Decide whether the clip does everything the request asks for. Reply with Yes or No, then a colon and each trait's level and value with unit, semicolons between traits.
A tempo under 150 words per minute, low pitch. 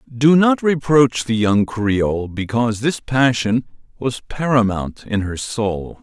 Yes: average, 140 wpm; low, 120 Hz